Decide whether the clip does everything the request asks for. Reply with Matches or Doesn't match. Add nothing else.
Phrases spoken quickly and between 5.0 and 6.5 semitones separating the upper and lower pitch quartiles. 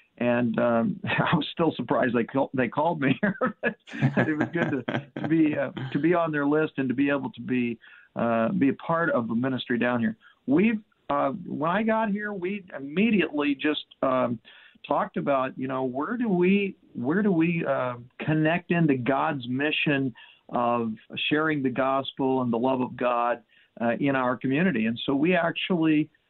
Doesn't match